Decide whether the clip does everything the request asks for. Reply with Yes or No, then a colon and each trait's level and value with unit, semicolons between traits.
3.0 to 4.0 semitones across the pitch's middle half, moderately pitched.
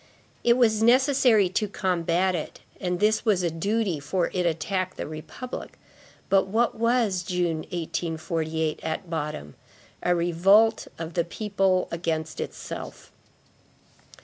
No: average, 4.4 semitones; medium, 180 Hz